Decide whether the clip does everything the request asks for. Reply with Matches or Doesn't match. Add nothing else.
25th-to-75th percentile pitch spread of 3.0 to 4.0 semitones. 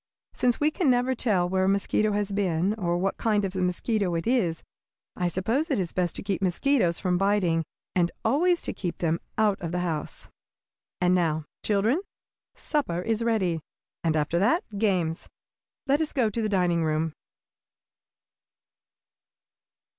Doesn't match